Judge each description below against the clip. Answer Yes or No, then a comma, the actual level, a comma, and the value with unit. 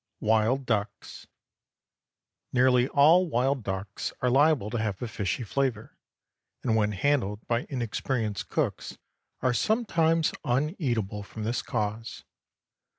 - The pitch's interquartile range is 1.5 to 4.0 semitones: No, average, 4.5 semitones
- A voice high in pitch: No, low, 120 Hz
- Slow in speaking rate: Yes, slow, 115 wpm